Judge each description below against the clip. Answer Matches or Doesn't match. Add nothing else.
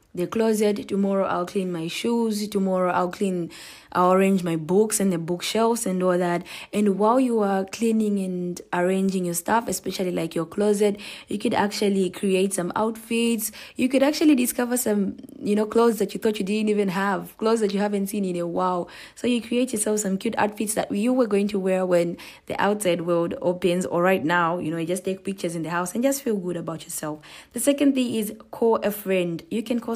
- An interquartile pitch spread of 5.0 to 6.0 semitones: Doesn't match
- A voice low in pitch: Doesn't match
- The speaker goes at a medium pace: Doesn't match